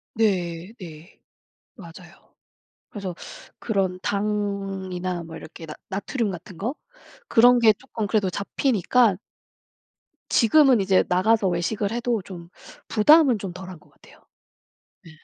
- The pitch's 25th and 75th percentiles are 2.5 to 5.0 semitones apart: Yes, average, 3.7 semitones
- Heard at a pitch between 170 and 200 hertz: Yes, high, 195 Hz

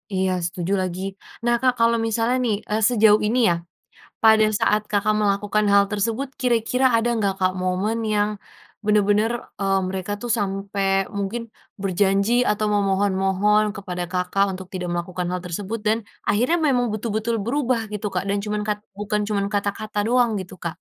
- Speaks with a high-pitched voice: Yes, high, 205 Hz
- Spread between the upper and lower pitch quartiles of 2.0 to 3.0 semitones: Yes, narrow, 2.5 semitones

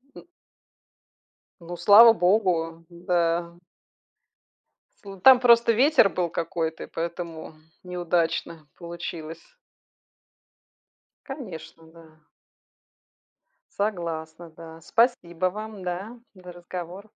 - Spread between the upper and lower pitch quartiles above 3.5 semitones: No, average, 3.1 semitones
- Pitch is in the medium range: Yes, medium, 175 Hz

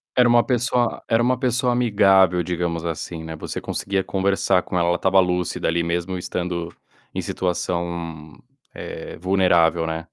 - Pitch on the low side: Yes, very low, 90 Hz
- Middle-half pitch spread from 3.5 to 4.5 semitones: No, narrow, 2.6 semitones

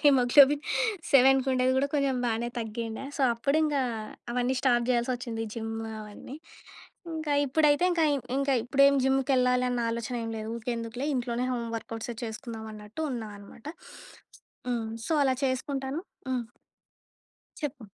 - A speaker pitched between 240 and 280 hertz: Yes, very high, 250 Hz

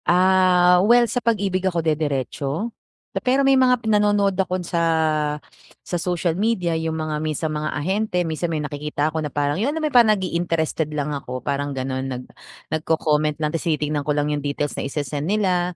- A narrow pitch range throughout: No, average, 4.2 semitones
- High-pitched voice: No, medium, 165 Hz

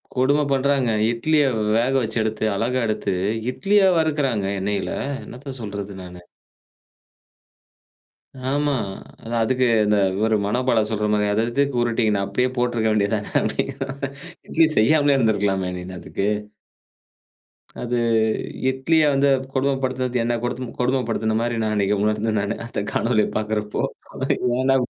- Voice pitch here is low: Yes, low, 120 Hz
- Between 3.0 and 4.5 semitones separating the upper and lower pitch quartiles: Yes, average, 3.9 semitones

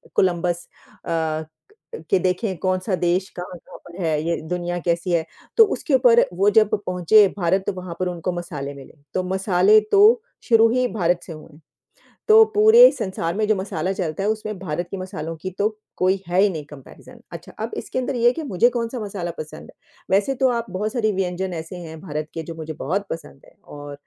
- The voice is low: No, medium, 185 Hz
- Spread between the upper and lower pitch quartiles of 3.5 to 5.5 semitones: Yes, average, 4.1 semitones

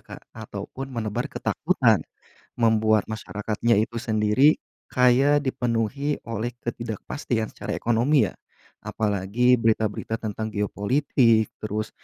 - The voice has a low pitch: Yes, low, 115 Hz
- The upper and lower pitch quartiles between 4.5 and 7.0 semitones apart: No, narrow, 2.4 semitones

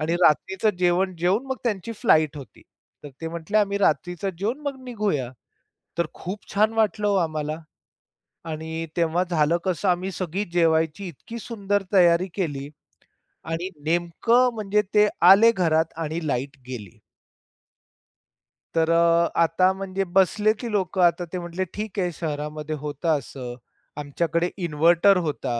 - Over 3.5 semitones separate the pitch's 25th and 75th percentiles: Yes, average, 3.9 semitones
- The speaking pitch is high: No, medium, 175 Hz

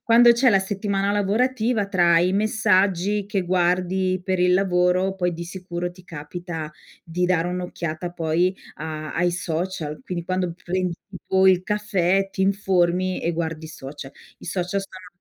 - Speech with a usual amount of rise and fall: No, narrow, 2.1 semitones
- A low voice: No, medium, 180 Hz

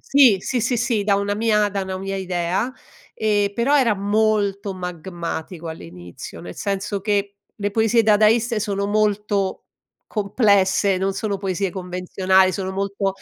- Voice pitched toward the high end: Yes, high, 200 Hz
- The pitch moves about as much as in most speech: No, narrow, 2.0 semitones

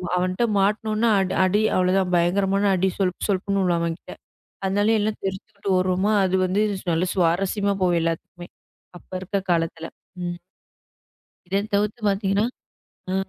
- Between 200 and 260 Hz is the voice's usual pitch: No, high, 190 Hz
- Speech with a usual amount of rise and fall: No, narrow, 2.1 semitones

